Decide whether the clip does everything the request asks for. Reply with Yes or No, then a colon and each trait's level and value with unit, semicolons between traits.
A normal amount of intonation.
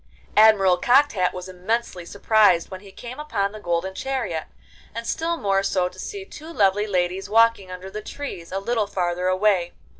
Yes: average, 3.9 semitones